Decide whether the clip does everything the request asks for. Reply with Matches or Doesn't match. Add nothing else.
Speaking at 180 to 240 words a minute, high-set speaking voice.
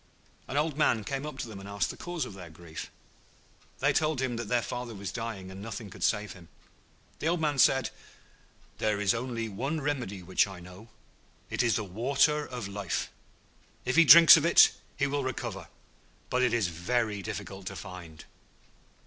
Doesn't match